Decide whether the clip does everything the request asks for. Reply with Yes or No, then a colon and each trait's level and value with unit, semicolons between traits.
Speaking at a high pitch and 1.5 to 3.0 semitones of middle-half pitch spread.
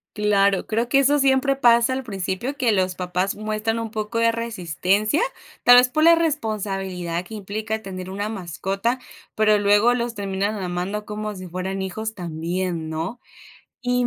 No: high, 210 Hz; average, 3.7 semitones